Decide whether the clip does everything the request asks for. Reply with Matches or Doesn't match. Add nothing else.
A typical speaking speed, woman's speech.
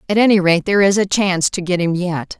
Doesn't match